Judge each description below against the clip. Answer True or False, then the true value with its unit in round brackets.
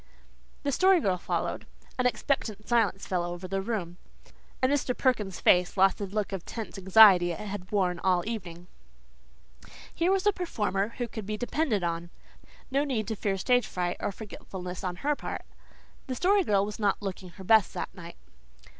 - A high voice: True (205 Hz)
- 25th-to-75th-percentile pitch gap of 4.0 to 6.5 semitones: True (4.9 semitones)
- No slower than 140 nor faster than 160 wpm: False (180 wpm)